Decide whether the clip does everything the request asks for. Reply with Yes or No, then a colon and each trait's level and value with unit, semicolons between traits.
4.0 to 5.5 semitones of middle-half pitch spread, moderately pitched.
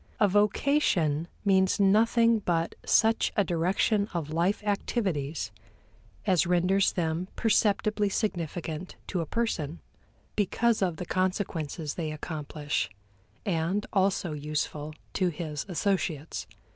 Yes: average, 4.3 semitones; medium, 180 Hz